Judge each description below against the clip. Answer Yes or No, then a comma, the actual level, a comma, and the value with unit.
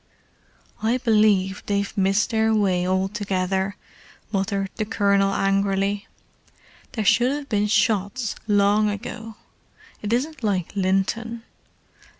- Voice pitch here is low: No, high, 205 Hz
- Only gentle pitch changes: Yes, narrow, 2.1 semitones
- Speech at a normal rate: No, slow, 110 wpm